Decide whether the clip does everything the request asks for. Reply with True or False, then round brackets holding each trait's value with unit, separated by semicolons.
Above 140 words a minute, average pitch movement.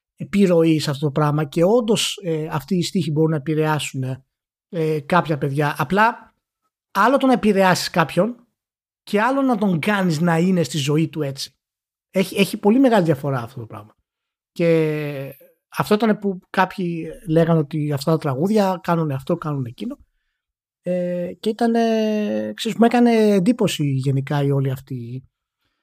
False (155 wpm; 5.8 semitones)